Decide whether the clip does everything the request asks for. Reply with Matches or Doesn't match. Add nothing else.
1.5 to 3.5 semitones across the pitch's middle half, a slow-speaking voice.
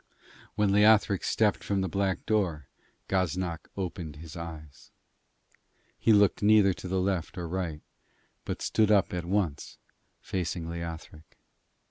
Matches